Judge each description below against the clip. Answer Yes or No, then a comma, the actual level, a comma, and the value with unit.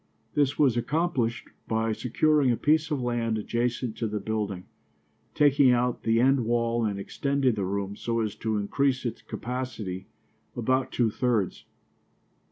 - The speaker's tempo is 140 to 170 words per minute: Yes, average, 150 wpm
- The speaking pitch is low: Yes, low, 120 Hz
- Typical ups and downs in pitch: Yes, average, 3.1 semitones